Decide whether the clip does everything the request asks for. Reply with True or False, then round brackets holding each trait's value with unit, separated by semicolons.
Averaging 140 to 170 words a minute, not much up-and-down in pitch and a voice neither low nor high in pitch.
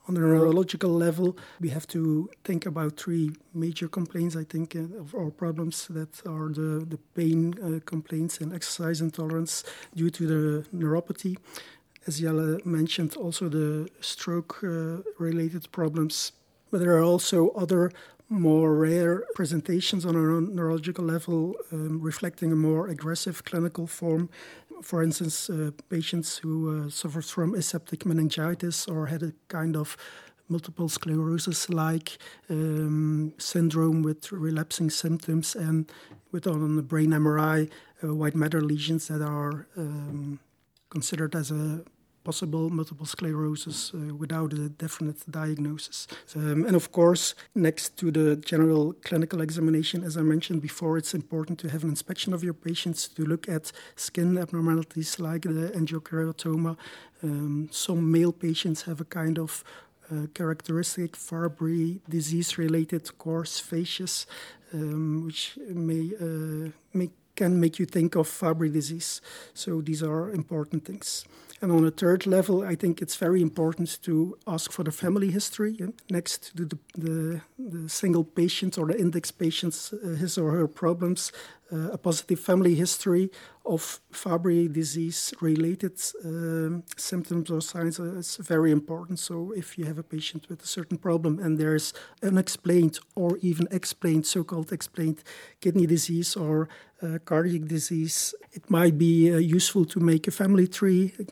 True (145 wpm; 1.7 semitones; 165 Hz)